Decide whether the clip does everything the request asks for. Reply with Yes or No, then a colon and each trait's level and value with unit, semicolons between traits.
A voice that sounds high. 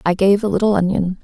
Yes: high, 195 Hz